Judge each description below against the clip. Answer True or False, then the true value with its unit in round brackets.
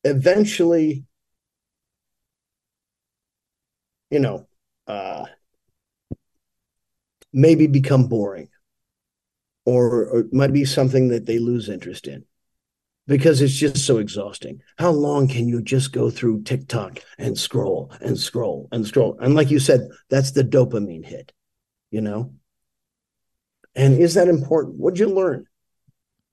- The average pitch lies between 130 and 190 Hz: True (135 Hz)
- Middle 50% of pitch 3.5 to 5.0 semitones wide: True (4.1 semitones)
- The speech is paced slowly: True (125 wpm)